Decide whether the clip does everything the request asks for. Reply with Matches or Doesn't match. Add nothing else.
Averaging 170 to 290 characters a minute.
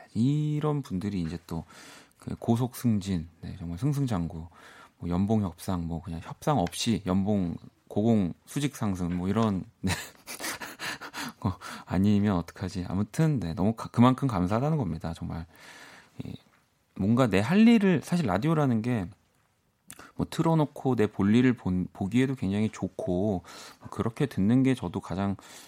Matches